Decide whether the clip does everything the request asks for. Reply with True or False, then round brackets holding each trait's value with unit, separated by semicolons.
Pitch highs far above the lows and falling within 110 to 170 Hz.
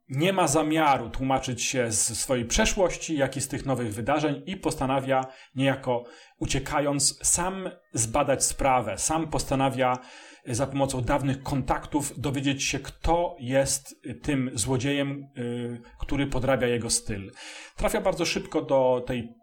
False (3.2 semitones; 135 Hz)